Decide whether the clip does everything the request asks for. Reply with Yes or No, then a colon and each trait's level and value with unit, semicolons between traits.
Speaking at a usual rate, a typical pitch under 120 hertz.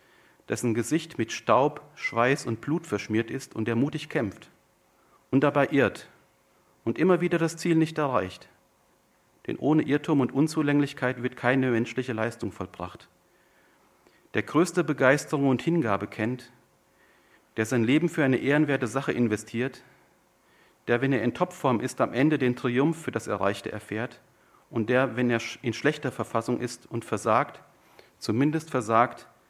No: average, 150 wpm; low, 125 Hz